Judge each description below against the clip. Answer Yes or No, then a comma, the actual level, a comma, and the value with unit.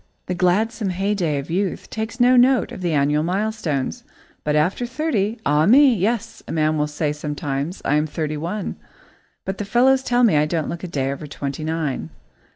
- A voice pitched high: No, medium, 175 Hz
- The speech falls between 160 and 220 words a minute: Yes, average, 190 wpm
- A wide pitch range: Yes, wide, 6.5 semitones